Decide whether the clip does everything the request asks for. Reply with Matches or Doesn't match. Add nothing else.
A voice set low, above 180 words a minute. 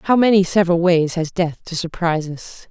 Doesn't match